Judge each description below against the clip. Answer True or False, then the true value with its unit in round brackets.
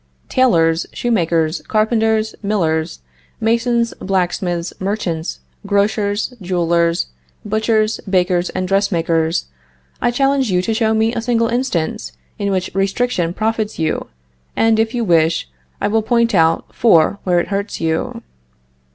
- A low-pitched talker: False (200 Hz)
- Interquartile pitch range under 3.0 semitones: False (4.6 semitones)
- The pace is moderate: False (125 wpm)